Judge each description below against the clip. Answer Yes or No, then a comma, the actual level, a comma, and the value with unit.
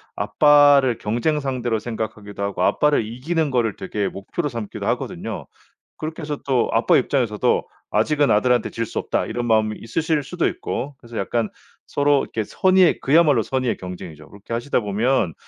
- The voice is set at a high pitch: No, low, 120 Hz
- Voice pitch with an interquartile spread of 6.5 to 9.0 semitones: No, average, 5.2 semitones